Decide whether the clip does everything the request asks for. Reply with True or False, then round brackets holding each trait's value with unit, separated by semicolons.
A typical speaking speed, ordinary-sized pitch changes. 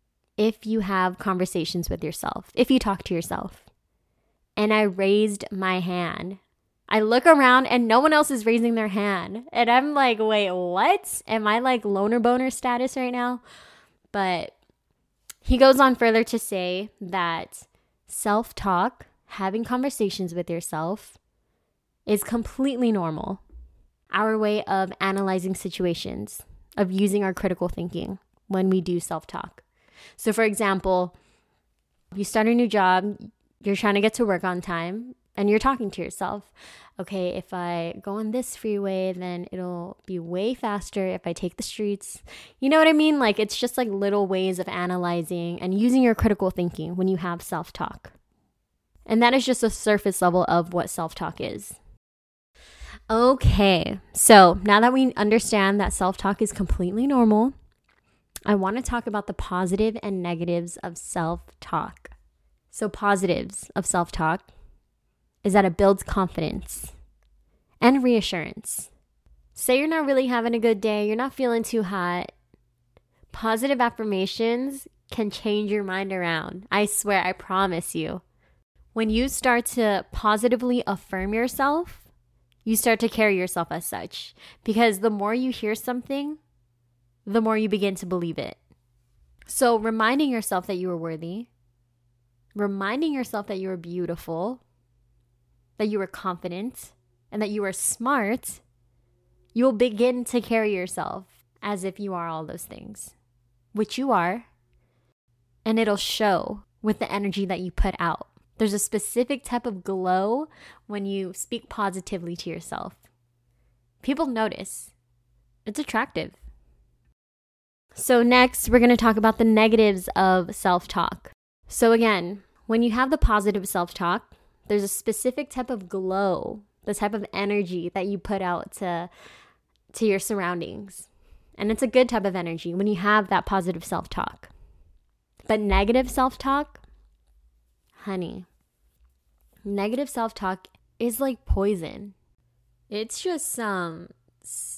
True (150 wpm; 4.4 semitones)